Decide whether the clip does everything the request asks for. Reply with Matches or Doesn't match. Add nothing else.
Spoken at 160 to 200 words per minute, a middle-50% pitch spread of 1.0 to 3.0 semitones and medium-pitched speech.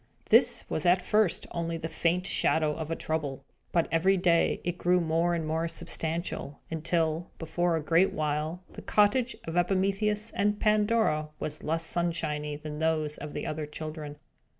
Matches